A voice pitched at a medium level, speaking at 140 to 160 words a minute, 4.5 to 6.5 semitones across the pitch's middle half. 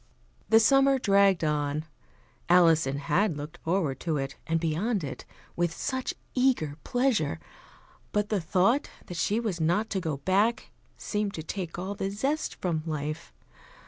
Yes: medium, 180 Hz; average, 150 wpm; average, 5.3 semitones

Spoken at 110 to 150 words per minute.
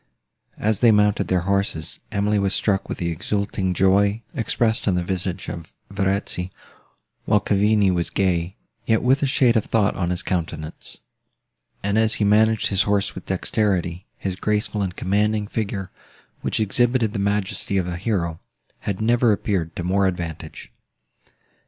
No: average, 160 wpm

